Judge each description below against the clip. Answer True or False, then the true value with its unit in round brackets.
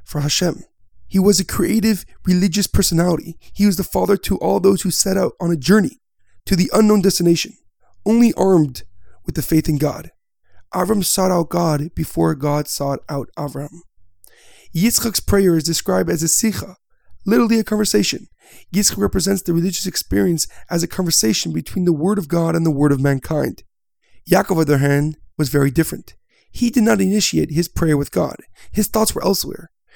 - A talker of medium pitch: True (170 Hz)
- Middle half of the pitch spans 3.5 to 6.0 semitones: True (4.8 semitones)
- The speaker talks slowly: False (180 wpm)